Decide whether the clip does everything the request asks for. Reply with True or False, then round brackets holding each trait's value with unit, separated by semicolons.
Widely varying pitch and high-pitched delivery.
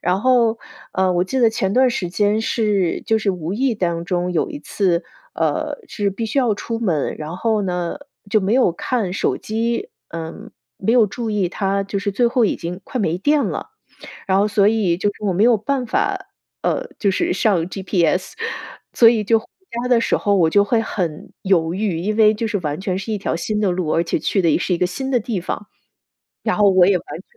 False (3.9 semitones; 200 Hz)